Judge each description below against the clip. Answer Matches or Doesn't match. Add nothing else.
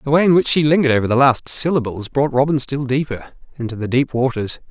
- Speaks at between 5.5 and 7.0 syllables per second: Matches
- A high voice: Doesn't match